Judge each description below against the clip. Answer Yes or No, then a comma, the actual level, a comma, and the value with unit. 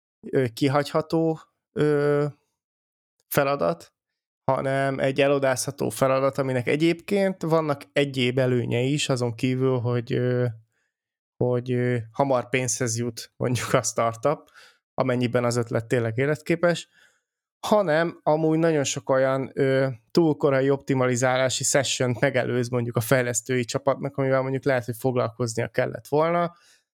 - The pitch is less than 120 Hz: No, low, 135 Hz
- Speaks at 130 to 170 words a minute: No, slow, 105 wpm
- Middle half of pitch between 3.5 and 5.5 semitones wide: No, average, 2.7 semitones